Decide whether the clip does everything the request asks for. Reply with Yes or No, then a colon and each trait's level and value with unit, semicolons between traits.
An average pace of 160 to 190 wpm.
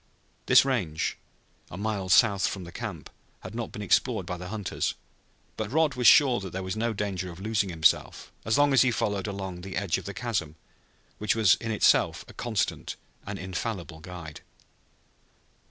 Yes: average, 180 wpm